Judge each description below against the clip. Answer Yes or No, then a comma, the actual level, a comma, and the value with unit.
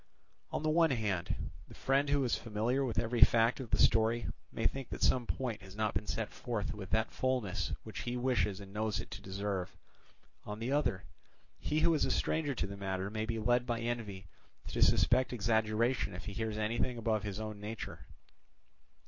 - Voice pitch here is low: Yes, low, 110 Hz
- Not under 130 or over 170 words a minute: No, average, 200 wpm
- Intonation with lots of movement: No, average, 3.0 semitones